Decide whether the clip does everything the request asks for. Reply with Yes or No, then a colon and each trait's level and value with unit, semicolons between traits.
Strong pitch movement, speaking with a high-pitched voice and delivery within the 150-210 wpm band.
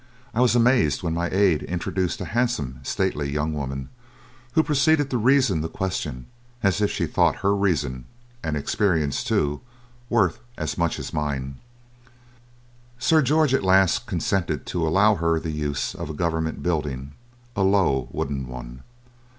No: wide, 6.0 semitones; very low, 85 Hz; average, 155 wpm